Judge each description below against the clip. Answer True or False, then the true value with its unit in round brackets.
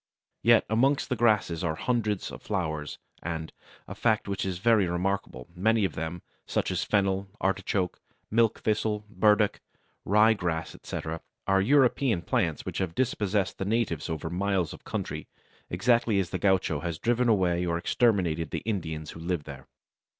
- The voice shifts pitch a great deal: False (4.4 semitones)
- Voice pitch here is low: True (95 Hz)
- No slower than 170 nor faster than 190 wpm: False (160 wpm)